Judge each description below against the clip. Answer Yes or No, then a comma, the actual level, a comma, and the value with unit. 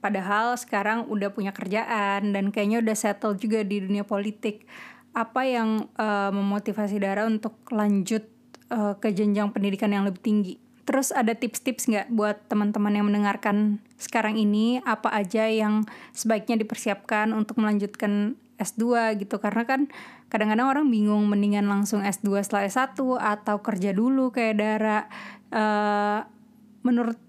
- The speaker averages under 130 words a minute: No, fast, 140 wpm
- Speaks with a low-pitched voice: No, high, 215 Hz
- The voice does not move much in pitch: Yes, narrow, 1.8 semitones